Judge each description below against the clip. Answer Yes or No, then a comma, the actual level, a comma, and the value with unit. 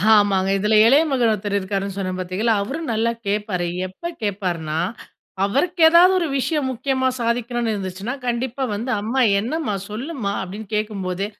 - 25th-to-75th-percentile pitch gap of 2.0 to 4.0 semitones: No, average, 4.9 semitones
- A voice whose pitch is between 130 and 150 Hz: No, high, 215 Hz